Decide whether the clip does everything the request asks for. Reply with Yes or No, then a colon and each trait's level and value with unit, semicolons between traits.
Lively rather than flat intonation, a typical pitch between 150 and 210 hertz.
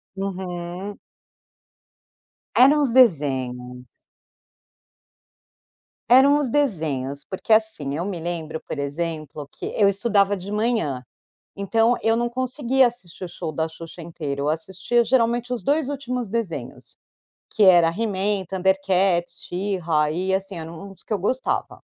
Yes: wide, 6.0 semitones; high, 190 Hz